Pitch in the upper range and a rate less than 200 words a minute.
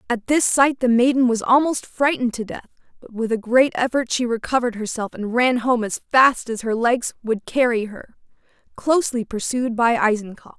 Yes: high, 240 Hz; average, 185 wpm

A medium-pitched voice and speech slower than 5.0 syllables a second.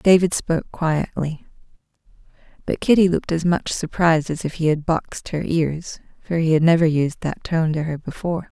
No: medium, 160 Hz; 5.2 syllables/s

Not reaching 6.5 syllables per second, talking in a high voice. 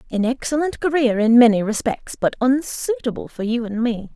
Yes: 5.2 syllables/s; high, 245 Hz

